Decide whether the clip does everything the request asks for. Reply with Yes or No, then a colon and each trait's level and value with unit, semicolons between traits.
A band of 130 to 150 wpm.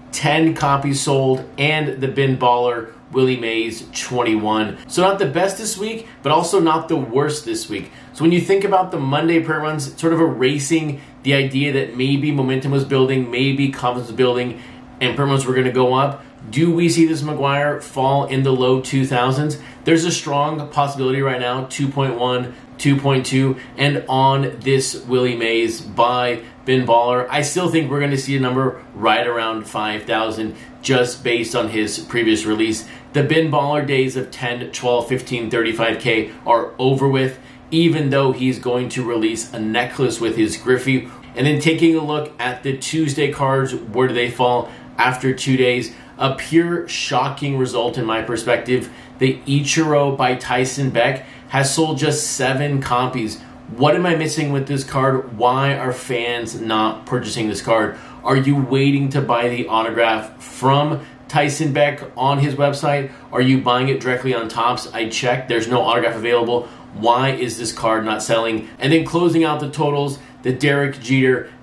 No: average, 175 wpm